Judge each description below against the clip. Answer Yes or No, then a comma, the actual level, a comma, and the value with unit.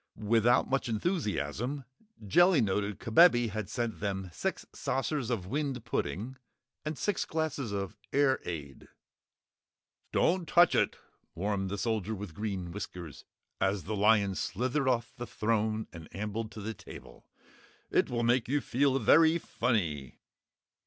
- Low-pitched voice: Yes, low, 110 Hz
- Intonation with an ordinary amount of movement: Yes, average, 4.9 semitones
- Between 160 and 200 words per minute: No, average, 140 wpm